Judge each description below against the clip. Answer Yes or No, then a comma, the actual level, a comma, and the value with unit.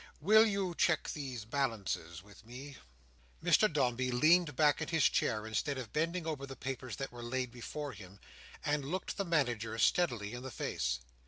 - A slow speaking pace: No, average, 175 wpm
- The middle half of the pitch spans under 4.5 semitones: No, average, 4.9 semitones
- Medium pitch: No, low, 130 Hz